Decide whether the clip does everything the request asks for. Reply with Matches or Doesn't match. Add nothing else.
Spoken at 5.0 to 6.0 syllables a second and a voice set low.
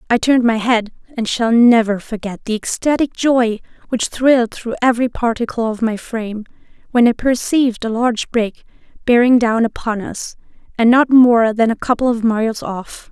Doesn't match